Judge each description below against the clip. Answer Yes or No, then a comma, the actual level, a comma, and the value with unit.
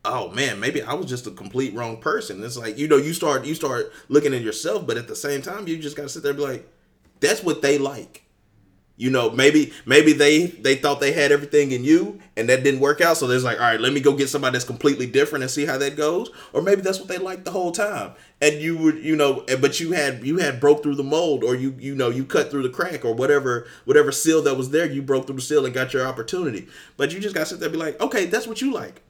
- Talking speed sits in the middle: No, fast, 280 wpm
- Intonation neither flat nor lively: Yes, average, 3.3 semitones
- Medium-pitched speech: Yes, medium, 145 Hz